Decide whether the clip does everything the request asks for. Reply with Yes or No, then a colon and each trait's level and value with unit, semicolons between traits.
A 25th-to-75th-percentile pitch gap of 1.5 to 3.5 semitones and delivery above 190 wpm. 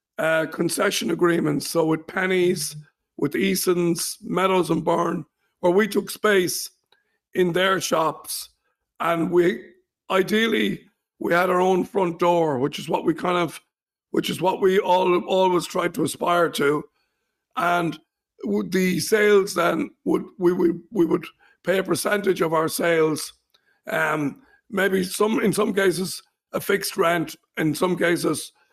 No: narrow, 2.4 semitones; average, 145 wpm